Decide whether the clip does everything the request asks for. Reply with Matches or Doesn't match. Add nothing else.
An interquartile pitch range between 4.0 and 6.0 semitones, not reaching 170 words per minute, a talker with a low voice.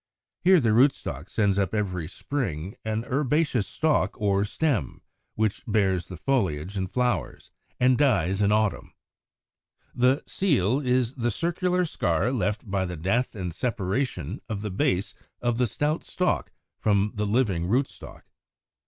Matches